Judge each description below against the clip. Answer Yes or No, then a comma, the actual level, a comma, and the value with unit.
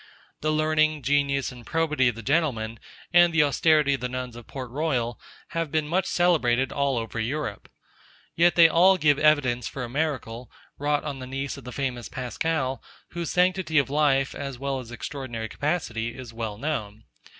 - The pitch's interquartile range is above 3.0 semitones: Yes, average, 4.1 semitones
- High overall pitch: No, medium, 140 Hz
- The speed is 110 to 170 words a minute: No, average, 180 wpm